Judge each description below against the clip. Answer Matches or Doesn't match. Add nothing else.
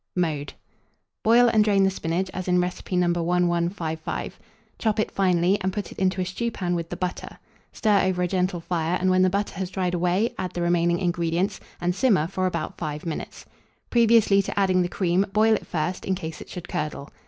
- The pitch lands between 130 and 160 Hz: Doesn't match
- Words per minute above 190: Matches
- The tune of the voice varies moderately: Doesn't match